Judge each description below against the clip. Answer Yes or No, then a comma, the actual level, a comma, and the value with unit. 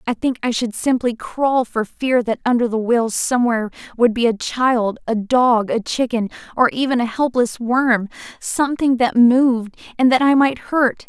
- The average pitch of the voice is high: Yes, high, 240 Hz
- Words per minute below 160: No, average, 180 wpm